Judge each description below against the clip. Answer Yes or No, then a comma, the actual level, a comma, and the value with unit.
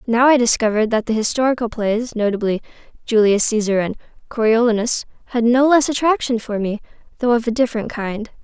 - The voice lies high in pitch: Yes, high, 230 Hz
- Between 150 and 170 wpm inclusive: Yes, average, 165 wpm